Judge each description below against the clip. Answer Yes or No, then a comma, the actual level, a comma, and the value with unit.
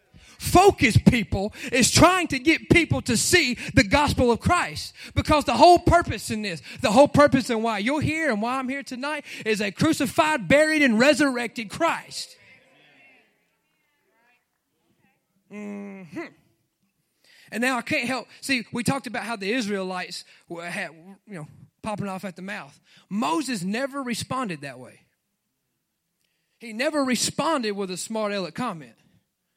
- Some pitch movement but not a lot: No, wide, 6.5 semitones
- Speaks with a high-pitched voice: Yes, high, 235 Hz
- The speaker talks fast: No, average, 150 wpm